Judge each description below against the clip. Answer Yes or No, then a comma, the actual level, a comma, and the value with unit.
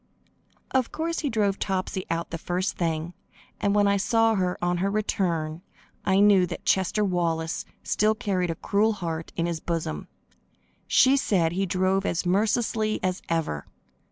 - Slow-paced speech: No, average, 160 wpm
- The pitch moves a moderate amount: Yes, average, 3.5 semitones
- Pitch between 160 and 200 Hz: Yes, medium, 185 Hz